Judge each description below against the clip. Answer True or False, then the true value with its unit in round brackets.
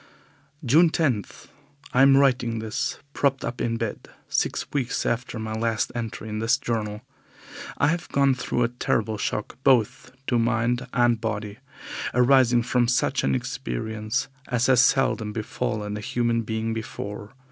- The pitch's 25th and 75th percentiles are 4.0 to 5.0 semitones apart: False (2.4 semitones)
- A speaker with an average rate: True (150 wpm)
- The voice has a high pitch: False (115 Hz)